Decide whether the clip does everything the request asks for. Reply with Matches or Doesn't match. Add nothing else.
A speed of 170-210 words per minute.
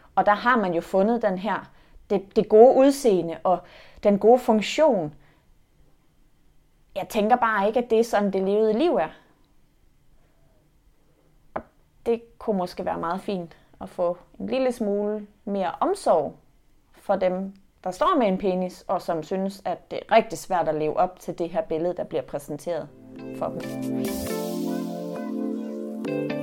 Doesn't match